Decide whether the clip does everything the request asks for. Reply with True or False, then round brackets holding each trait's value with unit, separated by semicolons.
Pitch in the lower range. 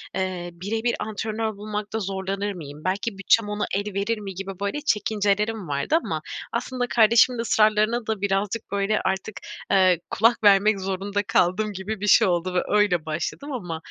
False (205 Hz)